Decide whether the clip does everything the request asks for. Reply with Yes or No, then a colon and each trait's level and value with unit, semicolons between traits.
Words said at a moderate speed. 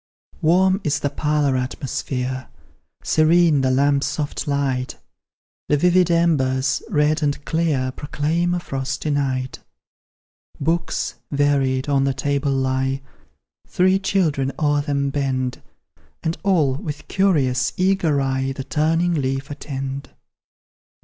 No: slow, 115 wpm